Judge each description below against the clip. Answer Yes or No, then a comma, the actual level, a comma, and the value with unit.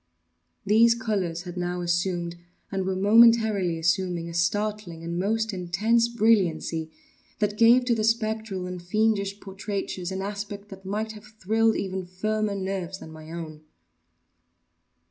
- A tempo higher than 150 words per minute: No, average, 140 wpm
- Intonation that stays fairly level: No, average, 3.5 semitones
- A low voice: No, high, 195 Hz